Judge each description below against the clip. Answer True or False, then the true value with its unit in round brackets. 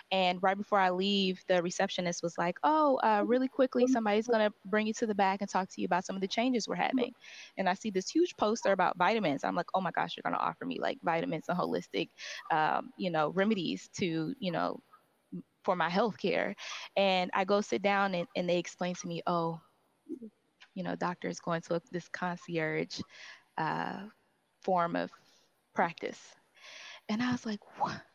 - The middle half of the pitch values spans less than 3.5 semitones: False (3.8 semitones)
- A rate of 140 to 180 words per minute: False (200 wpm)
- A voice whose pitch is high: True (195 Hz)